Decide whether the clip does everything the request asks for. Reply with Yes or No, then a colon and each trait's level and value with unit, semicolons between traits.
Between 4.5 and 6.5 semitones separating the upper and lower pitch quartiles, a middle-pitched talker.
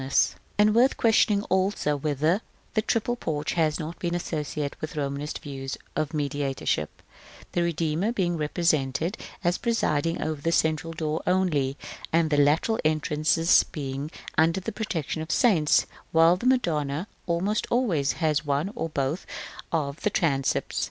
No: average, 3.6 semitones; medium, 160 Hz